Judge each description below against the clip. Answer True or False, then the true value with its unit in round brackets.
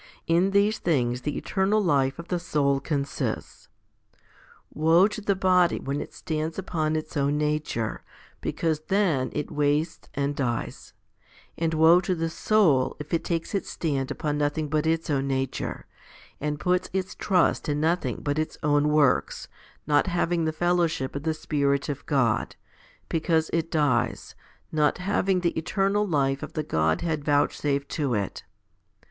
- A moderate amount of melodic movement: True (3.4 semitones)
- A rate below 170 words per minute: True (155 wpm)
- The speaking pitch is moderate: True (155 Hz)